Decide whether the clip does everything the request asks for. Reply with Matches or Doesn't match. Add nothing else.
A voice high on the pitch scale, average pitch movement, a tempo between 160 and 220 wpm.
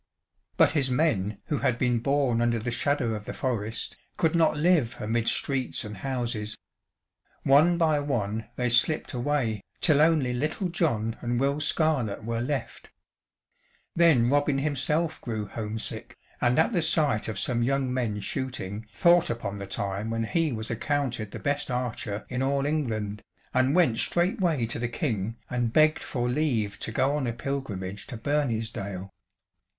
Doesn't match